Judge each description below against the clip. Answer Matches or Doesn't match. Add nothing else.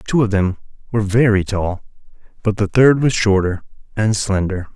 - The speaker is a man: Matches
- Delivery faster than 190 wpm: Doesn't match